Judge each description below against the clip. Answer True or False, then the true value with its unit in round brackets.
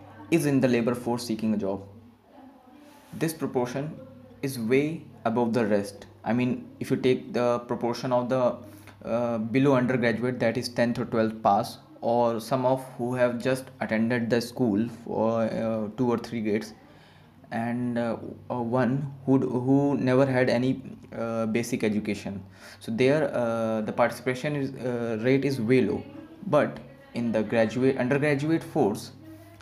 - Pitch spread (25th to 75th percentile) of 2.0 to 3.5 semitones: True (2.5 semitones)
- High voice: False (120 Hz)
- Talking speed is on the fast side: False (155 wpm)